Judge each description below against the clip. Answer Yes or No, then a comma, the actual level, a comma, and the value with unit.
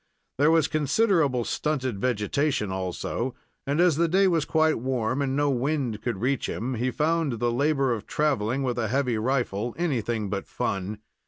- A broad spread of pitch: No, average, 4.7 semitones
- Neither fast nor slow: Yes, average, 170 wpm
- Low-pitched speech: Yes, low, 130 Hz